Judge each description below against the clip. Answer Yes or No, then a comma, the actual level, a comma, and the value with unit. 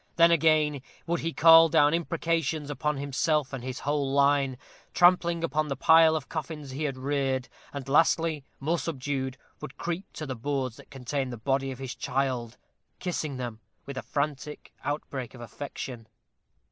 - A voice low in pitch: No, medium, 145 Hz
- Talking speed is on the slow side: No, average, 165 wpm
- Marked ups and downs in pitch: No, average, 3.2 semitones